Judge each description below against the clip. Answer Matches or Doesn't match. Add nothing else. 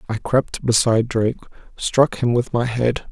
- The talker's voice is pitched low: Matches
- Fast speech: Doesn't match